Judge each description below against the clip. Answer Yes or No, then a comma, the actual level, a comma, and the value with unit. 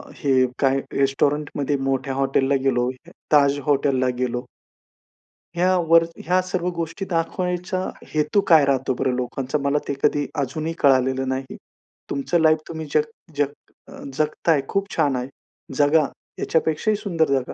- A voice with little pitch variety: No, average, 3.6 semitones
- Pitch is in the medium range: Yes, medium, 145 Hz